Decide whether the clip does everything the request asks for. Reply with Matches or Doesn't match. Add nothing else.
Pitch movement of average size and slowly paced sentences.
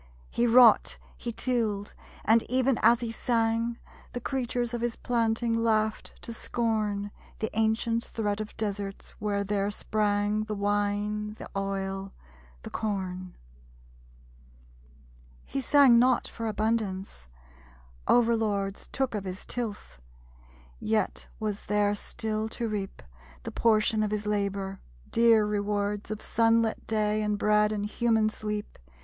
Doesn't match